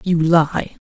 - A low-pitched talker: No, medium, 165 Hz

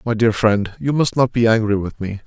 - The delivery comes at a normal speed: No, fast, 265 wpm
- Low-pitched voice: Yes, low, 110 Hz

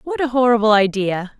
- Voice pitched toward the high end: Yes, high, 230 Hz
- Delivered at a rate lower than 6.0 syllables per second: Yes, 5.6 syllables/s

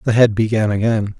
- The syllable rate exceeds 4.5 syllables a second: Yes, 5.6 syllables/s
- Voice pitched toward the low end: Yes, low, 110 Hz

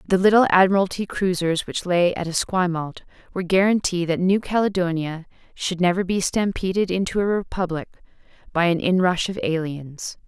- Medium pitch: Yes, medium, 180 Hz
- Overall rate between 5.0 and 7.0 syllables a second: Yes, 5.5 syllables/s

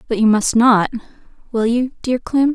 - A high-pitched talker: Yes, high, 235 Hz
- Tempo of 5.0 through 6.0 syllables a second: No, 4.8 syllables/s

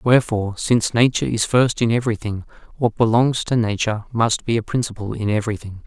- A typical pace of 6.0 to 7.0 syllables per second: Yes, 6.4 syllables/s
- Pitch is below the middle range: Yes, low, 115 Hz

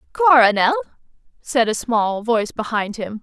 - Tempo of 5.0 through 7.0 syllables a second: No, 4.7 syllables/s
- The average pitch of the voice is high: Yes, high, 240 Hz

